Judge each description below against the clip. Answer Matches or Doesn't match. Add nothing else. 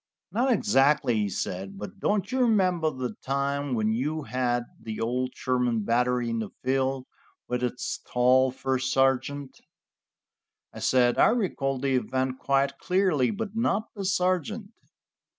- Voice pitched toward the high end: Doesn't match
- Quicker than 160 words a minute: Doesn't match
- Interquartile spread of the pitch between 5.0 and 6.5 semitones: Matches